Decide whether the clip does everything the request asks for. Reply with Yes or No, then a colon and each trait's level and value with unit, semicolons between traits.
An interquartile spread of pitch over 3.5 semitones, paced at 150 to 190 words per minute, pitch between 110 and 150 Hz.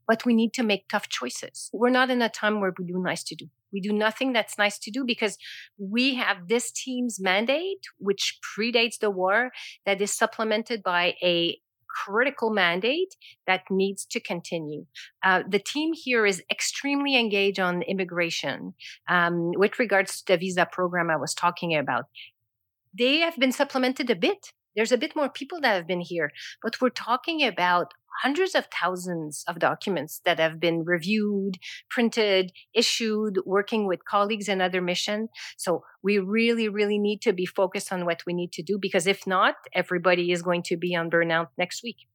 No: average, 4.6 semitones; average, 180 wpm; high, 200 Hz